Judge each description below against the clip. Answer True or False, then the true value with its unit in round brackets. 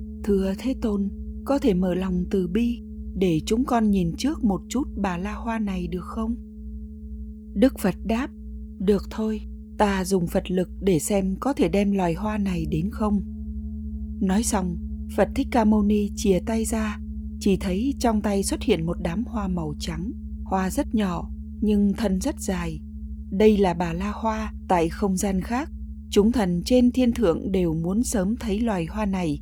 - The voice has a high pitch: True (195 Hz)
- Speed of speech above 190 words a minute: False (185 wpm)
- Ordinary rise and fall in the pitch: True (4.9 semitones)